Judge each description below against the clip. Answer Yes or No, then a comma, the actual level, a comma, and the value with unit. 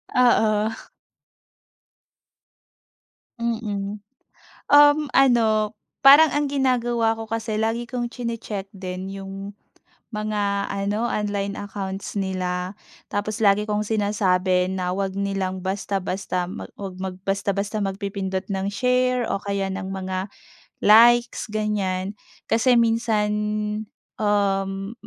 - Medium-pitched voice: No, high, 205 Hz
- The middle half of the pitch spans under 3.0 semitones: Yes, narrow, 2.6 semitones